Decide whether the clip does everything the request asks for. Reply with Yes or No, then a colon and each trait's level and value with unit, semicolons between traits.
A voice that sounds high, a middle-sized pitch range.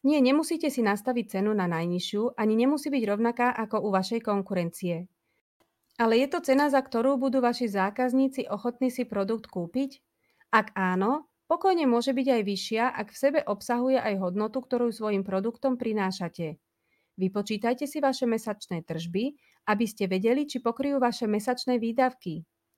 Yes: high, 230 Hz; average, 4.6 semitones